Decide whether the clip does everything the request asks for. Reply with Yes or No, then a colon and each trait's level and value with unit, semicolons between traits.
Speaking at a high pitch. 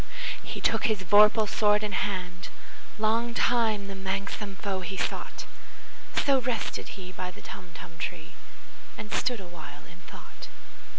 Yes: high, 200 Hz